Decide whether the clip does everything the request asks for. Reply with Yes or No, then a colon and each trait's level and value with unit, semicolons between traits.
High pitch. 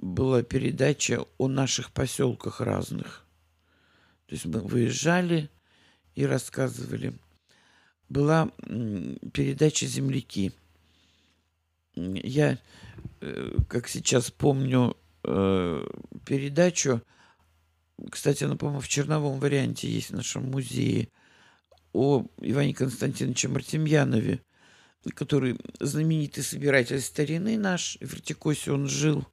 No: low, 130 Hz